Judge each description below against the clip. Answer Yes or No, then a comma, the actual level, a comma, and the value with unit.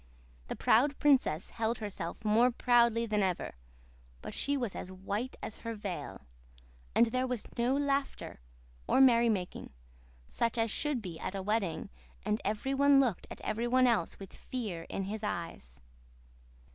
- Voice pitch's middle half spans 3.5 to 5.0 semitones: Yes, average, 4.3 semitones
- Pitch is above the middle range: Yes, high, 225 Hz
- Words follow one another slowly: No, average, 160 wpm